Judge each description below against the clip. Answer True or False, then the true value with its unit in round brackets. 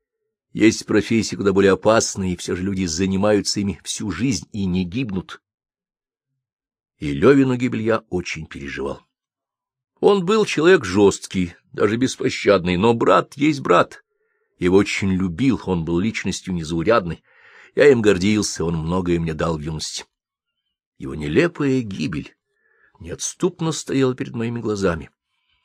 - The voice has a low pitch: True (105 Hz)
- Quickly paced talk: False (130 wpm)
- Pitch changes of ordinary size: False (7.0 semitones)